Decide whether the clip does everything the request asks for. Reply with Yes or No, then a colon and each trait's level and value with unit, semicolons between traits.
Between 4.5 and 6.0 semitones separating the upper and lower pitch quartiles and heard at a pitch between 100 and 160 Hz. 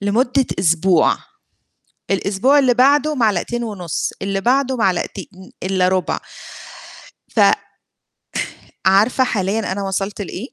No: average, 4.8 semitones; high, 205 Hz